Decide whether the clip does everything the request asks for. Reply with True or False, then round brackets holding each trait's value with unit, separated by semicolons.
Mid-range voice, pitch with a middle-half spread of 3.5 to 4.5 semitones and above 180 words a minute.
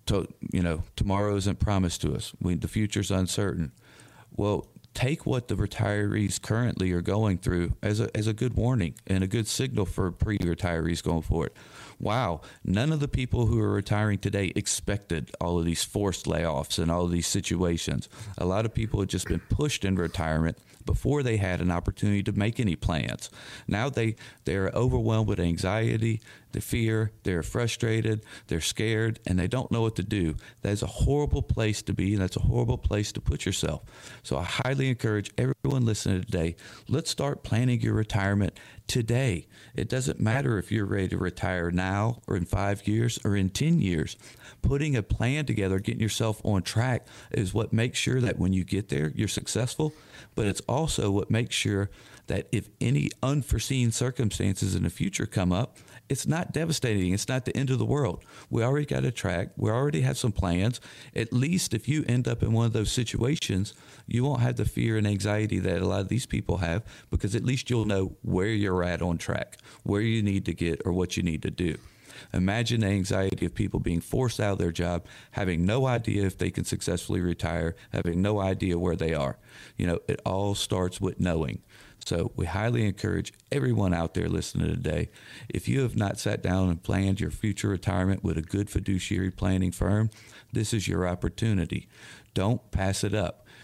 False (105 Hz; 4.0 semitones; 195 wpm)